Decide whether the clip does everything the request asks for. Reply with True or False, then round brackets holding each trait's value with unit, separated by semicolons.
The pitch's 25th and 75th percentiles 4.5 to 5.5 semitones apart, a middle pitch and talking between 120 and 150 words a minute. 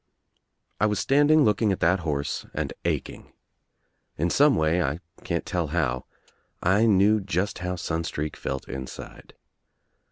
False (5.0 semitones; 90 Hz; 140 wpm)